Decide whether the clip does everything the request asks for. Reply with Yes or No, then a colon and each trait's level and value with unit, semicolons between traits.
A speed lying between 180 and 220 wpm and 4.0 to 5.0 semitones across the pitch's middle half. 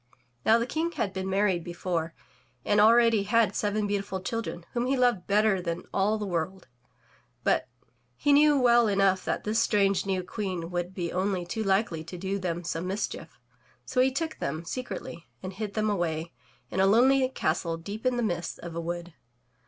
Yes: average, 185 wpm; average, 4.4 semitones